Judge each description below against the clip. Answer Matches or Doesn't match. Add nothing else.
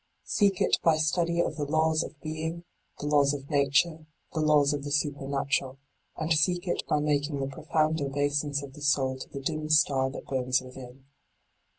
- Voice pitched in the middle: Matches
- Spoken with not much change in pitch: Matches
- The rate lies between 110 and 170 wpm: Doesn't match